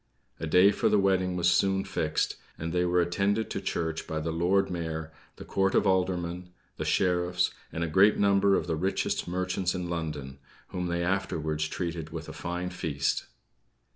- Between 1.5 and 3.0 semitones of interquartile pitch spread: Yes, narrow, 2.5 semitones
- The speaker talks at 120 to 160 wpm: No, average, 180 wpm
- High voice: No, very low, 90 Hz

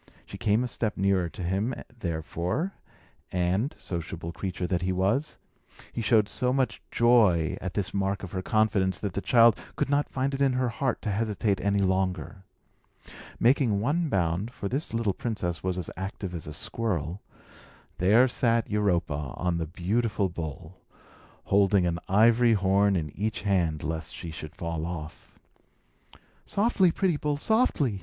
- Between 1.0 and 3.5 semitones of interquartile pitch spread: No, average, 4.9 semitones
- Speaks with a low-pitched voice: Yes, low, 100 Hz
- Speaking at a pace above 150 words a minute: Yes, average, 160 wpm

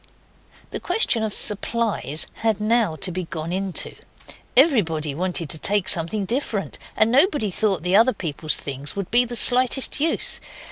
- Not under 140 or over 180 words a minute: Yes, average, 155 wpm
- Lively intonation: Yes, wide, 5.8 semitones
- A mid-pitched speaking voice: No, high, 205 Hz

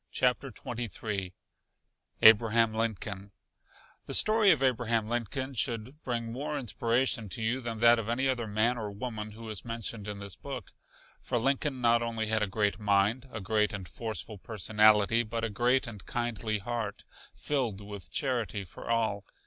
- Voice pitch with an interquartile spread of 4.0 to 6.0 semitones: No, narrow, 2.4 semitones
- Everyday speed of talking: Yes, average, 165 wpm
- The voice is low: Yes, low, 115 Hz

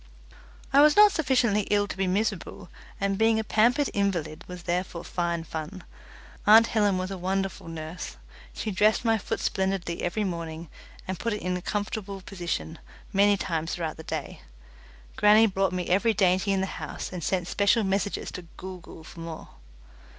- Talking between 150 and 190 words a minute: Yes, average, 175 wpm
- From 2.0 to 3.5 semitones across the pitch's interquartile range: Yes, average, 3.0 semitones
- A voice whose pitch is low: No, high, 195 Hz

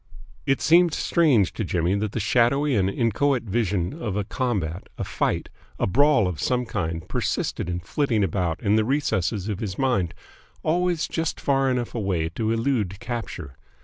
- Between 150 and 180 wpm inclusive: Yes, average, 170 wpm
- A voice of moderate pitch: No, low, 110 Hz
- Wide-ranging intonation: Yes, wide, 6.3 semitones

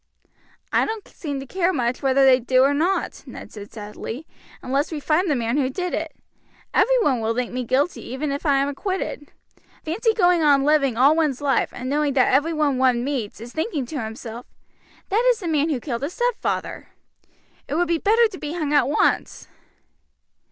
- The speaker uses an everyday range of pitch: Yes, average, 4.3 semitones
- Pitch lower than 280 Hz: No, very high, 285 Hz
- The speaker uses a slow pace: No, average, 195 wpm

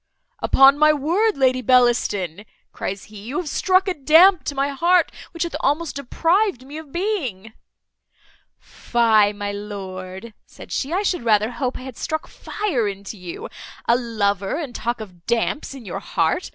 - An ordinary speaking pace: Yes, average, 165 wpm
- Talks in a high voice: Yes, very high, 255 Hz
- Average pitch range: No, wide, 7.0 semitones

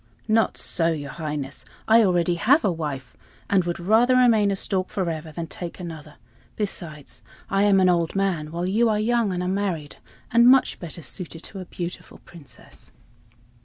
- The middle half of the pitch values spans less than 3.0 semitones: No, average, 4.0 semitones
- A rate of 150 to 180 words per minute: Yes, average, 170 wpm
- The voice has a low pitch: No, medium, 180 Hz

